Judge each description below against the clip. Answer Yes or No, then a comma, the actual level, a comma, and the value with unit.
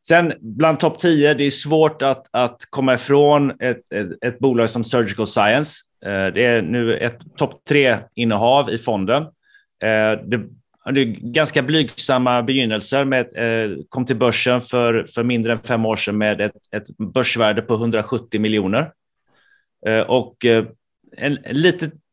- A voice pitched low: Yes, low, 120 Hz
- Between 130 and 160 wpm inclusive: Yes, average, 145 wpm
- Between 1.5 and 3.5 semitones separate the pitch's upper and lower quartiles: No, average, 3.9 semitones